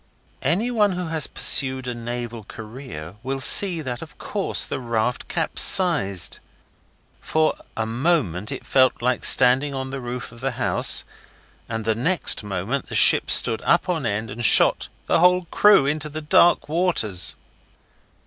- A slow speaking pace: No, average, 155 wpm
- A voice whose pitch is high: No, low, 130 Hz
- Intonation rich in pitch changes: Yes, wide, 5.8 semitones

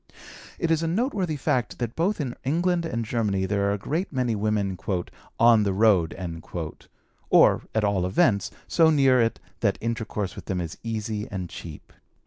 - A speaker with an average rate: Yes, average, 170 wpm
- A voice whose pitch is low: Yes, low, 110 Hz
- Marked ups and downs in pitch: Yes, wide, 6.1 semitones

